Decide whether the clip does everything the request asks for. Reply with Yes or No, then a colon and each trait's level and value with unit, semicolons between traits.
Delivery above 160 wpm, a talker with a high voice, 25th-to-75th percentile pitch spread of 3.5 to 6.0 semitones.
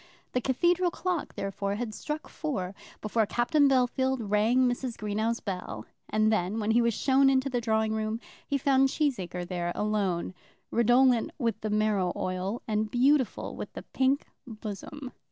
No: average, 155 wpm; high, 230 Hz; average, 4.0 semitones